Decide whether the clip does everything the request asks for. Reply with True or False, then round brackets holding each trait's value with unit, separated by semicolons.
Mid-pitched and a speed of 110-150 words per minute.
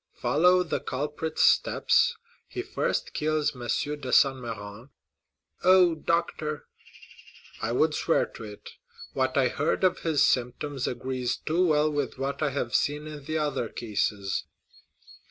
True (145 Hz; 140 wpm)